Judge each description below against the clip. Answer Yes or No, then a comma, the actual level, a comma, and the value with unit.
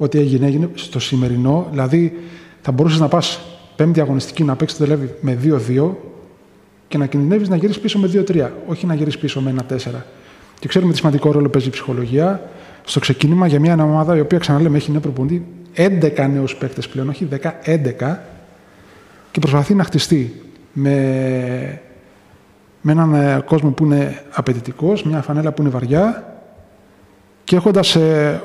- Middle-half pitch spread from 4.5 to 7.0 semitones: No, average, 3.5 semitones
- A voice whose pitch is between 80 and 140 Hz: No, medium, 150 Hz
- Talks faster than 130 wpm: Yes, average, 160 wpm